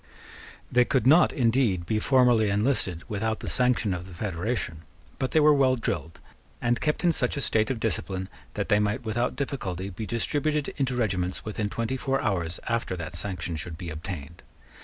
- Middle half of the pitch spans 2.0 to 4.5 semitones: No, wide, 5.6 semitones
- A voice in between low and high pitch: No, low, 110 Hz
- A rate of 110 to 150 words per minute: No, average, 180 wpm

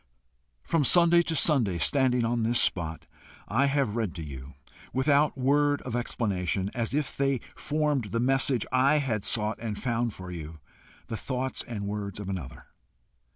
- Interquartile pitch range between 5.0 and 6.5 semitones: Yes, wide, 5.4 semitones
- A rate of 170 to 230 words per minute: No, average, 160 wpm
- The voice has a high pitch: No, low, 120 Hz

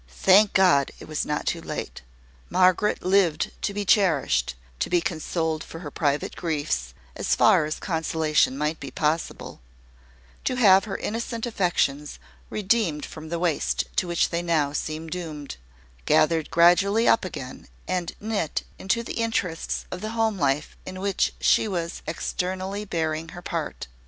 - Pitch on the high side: No, medium, 170 Hz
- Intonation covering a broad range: No, average, 4.0 semitones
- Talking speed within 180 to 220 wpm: No, average, 155 wpm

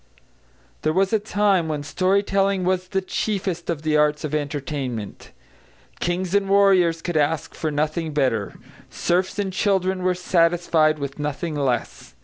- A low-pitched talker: No, medium, 170 Hz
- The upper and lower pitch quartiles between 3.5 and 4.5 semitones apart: Yes, average, 4.0 semitones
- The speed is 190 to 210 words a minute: No, average, 150 wpm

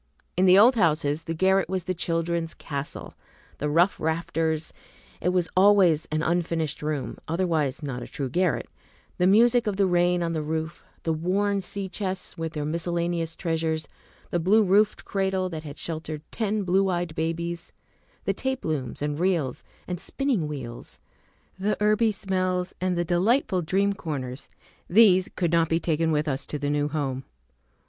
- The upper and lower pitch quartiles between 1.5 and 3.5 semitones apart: Yes, average, 3.2 semitones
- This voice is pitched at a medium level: Yes, medium, 170 Hz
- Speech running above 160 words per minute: Yes, average, 170 wpm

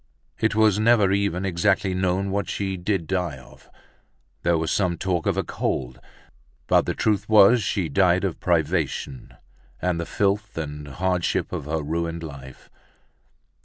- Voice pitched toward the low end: Yes, very low, 90 Hz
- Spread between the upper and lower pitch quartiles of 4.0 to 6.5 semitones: No, average, 3.2 semitones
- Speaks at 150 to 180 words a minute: Yes, average, 160 wpm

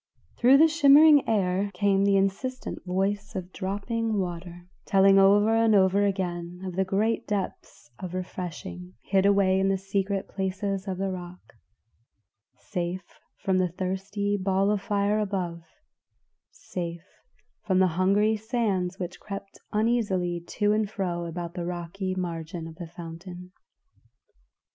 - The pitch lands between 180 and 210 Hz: Yes, high, 190 Hz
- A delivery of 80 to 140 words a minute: Yes, slow, 135 wpm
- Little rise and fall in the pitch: Yes, narrow, 2.3 semitones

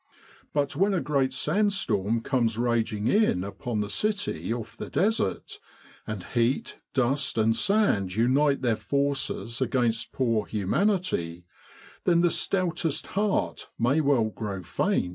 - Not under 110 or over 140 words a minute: Yes, slow, 135 wpm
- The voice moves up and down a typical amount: No, wide, 6.4 semitones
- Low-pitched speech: Yes, low, 125 Hz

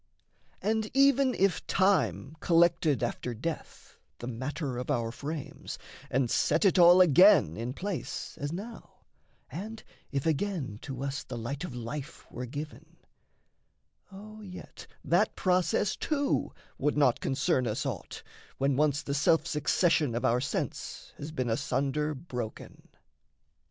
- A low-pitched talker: No, medium, 150 Hz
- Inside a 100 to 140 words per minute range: Yes, slow, 135 wpm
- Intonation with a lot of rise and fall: Yes, wide, 6.0 semitones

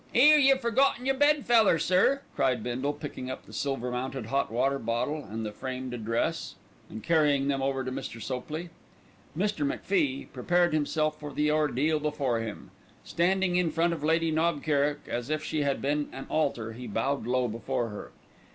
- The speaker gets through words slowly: No, average, 180 wpm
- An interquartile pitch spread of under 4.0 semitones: No, average, 4.5 semitones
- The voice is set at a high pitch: No, medium, 145 Hz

